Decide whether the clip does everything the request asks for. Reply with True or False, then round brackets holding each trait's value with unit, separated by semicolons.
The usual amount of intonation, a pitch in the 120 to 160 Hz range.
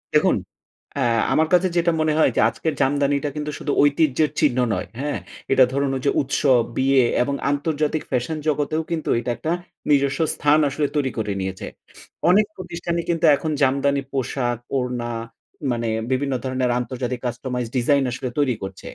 True (3.1 semitones; 140 Hz)